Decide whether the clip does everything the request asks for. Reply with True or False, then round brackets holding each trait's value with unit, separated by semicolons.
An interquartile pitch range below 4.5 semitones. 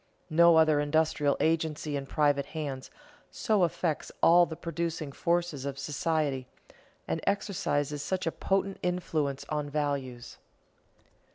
True (3.0 semitones)